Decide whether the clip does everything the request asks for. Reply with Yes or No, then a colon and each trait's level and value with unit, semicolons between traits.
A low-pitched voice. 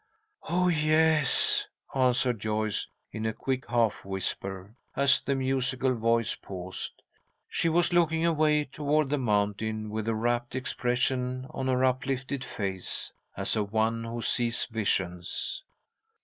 Yes: low, 125 Hz